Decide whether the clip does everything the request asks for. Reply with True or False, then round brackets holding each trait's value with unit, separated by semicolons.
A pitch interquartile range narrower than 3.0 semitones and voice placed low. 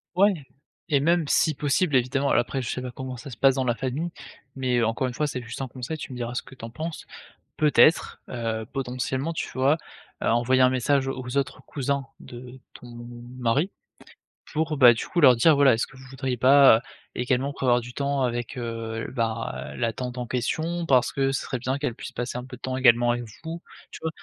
True (2.5 semitones; 130 Hz)